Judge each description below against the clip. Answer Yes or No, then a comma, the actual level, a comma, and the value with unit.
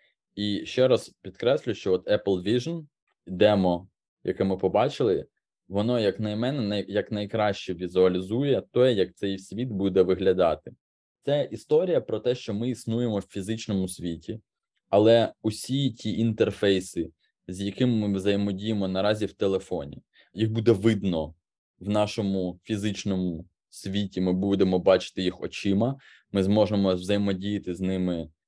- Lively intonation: No, average, 3.3 semitones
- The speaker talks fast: No, average, 130 wpm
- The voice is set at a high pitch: No, low, 100 Hz